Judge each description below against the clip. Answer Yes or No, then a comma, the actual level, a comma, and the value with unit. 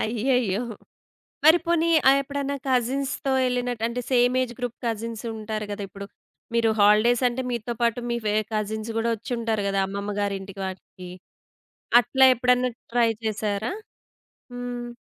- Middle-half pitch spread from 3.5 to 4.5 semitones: No, average, 2.8 semitones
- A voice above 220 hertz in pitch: Yes, high, 235 Hz